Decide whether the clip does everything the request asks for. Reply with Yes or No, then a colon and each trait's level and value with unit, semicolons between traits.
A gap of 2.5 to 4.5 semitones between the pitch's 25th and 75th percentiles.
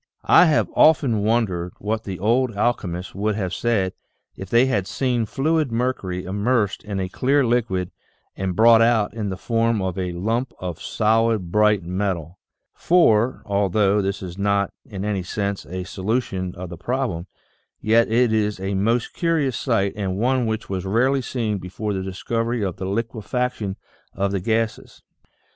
Yes: average, 3.6 semitones